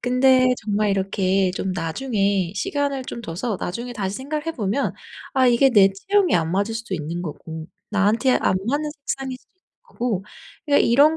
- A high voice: Yes, high, 225 Hz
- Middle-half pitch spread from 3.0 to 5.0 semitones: No, wide, 5.6 semitones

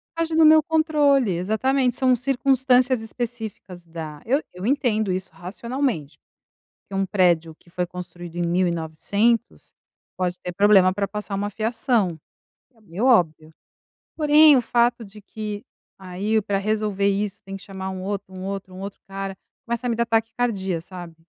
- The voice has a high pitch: Yes, high, 205 Hz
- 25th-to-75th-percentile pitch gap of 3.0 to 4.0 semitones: No, average, 4.6 semitones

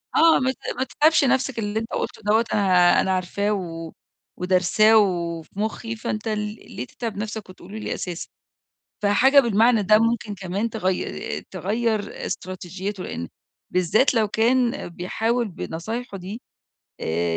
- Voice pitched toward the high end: Yes, high, 210 Hz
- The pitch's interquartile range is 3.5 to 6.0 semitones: Yes, average, 3.9 semitones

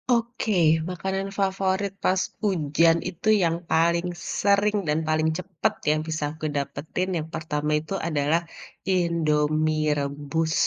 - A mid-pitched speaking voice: Yes, medium, 165 Hz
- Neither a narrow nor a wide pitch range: Yes, average, 3.5 semitones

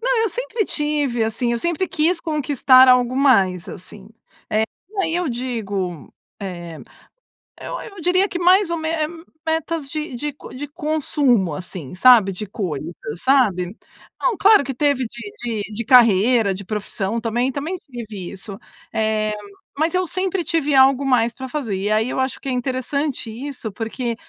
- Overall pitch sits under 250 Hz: No, very high, 255 Hz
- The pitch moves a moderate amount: No, wide, 6.0 semitones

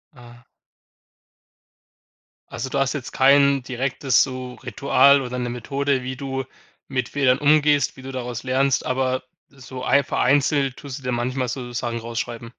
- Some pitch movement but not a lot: No, narrow, 1.8 semitones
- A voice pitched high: No, low, 130 Hz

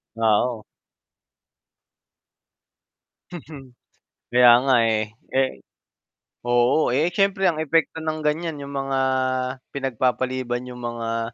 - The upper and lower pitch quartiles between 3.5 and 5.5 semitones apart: Yes, average, 4.3 semitones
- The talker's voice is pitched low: Yes, low, 130 Hz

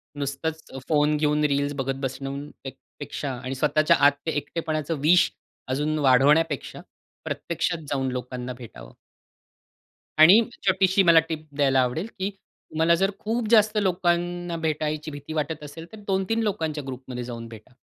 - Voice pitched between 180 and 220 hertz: No, medium, 155 Hz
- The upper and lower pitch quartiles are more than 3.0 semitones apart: Yes, average, 3.7 semitones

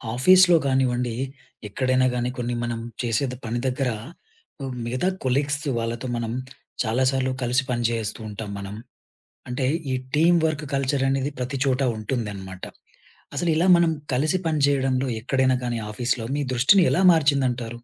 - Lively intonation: No, average, 2.9 semitones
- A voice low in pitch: Yes, low, 130 Hz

